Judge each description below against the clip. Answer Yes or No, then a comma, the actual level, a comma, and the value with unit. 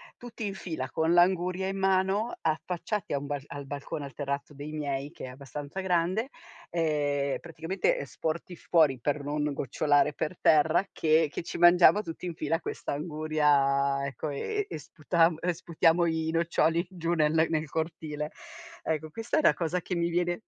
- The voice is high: No, medium, 160 Hz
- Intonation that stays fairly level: No, average, 3.2 semitones